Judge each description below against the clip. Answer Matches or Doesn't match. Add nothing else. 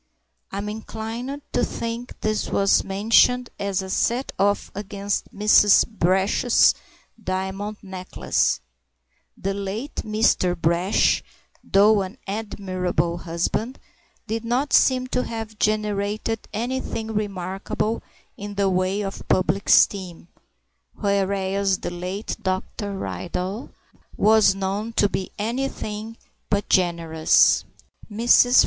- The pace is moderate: Doesn't match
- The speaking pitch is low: Doesn't match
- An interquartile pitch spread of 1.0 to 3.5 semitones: Matches